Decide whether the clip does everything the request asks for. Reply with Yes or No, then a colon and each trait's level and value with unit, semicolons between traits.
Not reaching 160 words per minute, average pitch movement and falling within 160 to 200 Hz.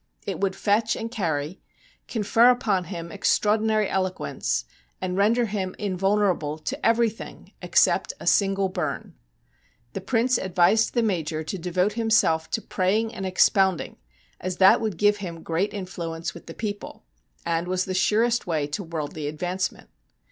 Yes: average, 150 wpm; average, 3.8 semitones; high, 190 Hz